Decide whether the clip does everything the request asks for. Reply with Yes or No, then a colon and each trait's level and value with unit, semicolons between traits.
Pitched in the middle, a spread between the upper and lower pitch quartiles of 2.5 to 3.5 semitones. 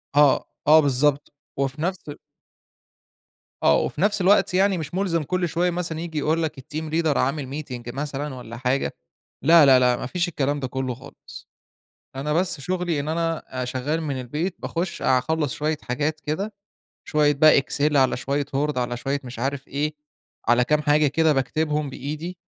Yes: medium, 150 Hz; average, 3.2 semitones